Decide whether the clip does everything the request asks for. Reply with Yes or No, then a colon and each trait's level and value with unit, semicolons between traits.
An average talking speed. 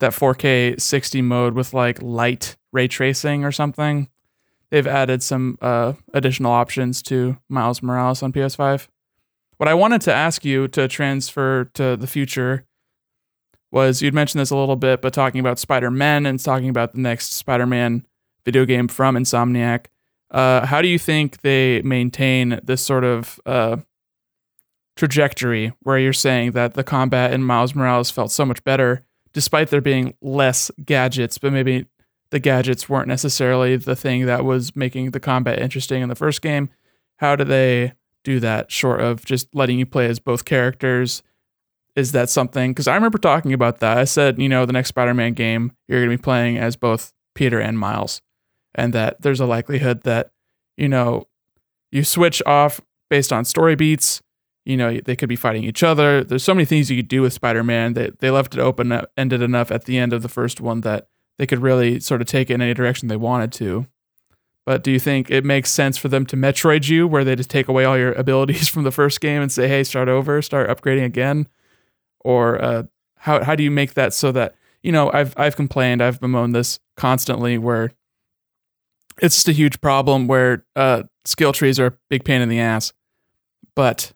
Yes: average, 195 wpm